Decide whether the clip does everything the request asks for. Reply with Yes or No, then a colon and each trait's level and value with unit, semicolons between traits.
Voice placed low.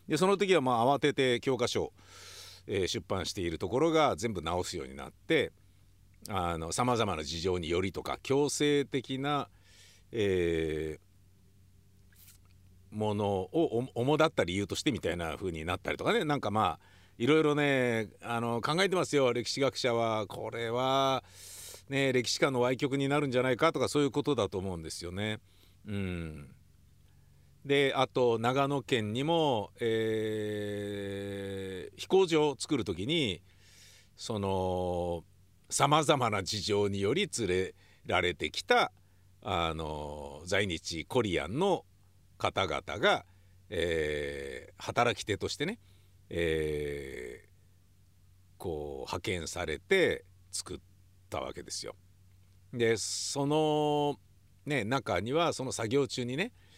Yes: low, 100 Hz